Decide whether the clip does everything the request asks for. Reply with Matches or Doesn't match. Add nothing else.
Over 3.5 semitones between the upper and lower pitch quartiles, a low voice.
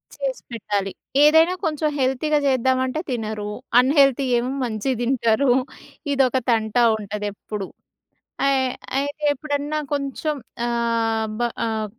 Doesn't match